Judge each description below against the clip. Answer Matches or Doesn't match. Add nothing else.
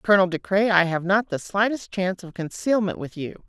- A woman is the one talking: Matches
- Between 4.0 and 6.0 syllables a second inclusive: Matches